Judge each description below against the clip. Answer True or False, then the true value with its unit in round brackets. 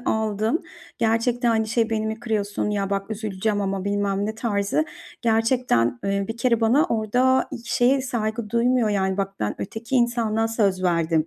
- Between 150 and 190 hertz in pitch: False (220 Hz)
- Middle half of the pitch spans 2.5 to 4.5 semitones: True (2.8 semitones)